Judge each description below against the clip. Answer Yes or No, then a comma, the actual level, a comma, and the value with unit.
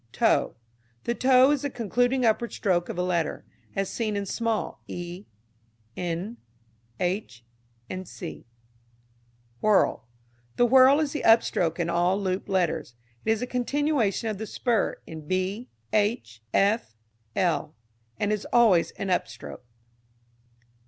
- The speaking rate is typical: No, slow, 130 wpm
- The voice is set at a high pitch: Yes, high, 205 Hz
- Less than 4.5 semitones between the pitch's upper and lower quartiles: No, average, 5.2 semitones